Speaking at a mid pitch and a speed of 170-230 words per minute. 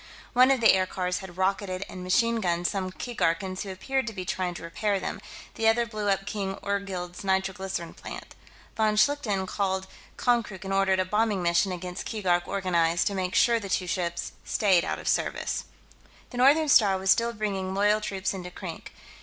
No: high, 195 Hz; average, 185 wpm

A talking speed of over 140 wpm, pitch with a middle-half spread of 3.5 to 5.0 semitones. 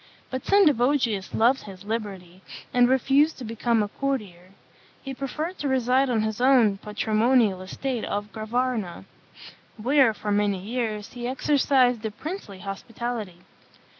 No: slow, 135 wpm; average, 4.1 semitones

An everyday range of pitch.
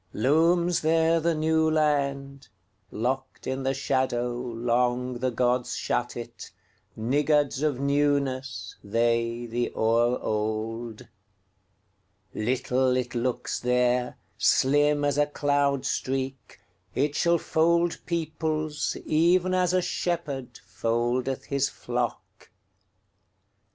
Yes: average, 3.9 semitones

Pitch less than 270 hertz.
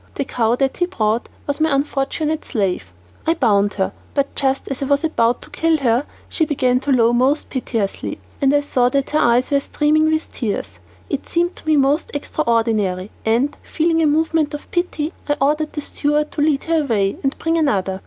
No: very high, 280 Hz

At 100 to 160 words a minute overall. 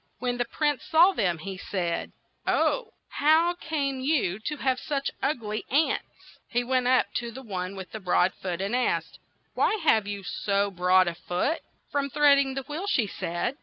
No: average, 185 wpm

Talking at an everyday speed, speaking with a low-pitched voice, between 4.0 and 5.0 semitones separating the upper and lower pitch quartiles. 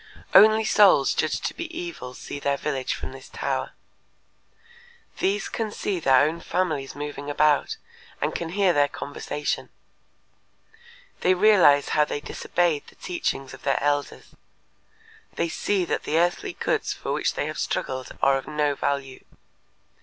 No: average, 150 wpm; medium, 150 Hz; average, 4.7 semitones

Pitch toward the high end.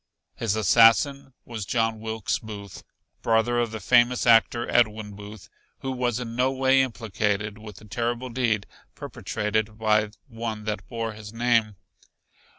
No: low, 115 Hz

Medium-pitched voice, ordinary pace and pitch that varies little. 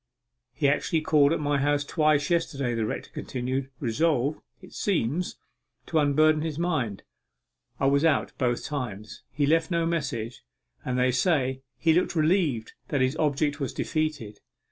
No: medium, 145 Hz; average, 155 wpm; average, 3.6 semitones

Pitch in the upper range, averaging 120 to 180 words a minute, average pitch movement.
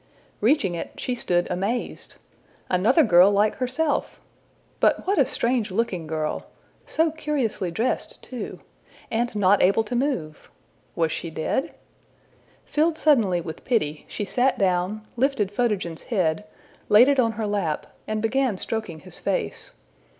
No: high, 215 Hz; average, 140 wpm; wide, 5.8 semitones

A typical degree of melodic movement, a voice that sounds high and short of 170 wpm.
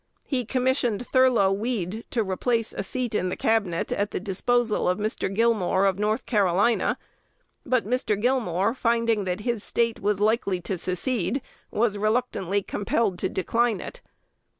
Yes: average, 3.6 semitones; high, 215 Hz; average, 150 wpm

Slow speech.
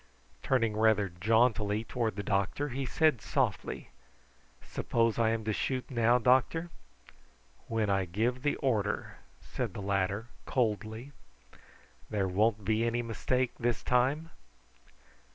Yes: slow, 125 wpm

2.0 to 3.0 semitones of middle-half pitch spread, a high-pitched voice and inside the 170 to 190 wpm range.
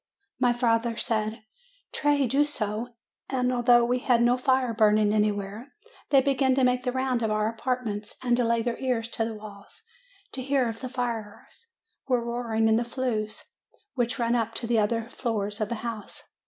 Yes: narrow, 2.4 semitones; high, 235 Hz; average, 185 wpm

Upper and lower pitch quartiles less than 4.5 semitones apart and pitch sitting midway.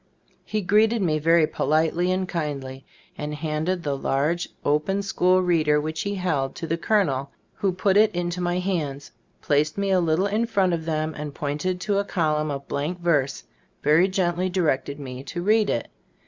Yes: average, 3.8 semitones; medium, 170 Hz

